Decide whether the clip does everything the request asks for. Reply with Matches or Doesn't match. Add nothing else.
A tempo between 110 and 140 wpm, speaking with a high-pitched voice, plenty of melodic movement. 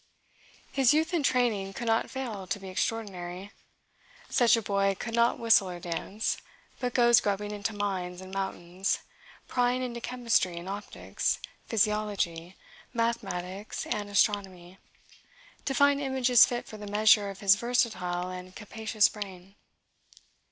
Doesn't match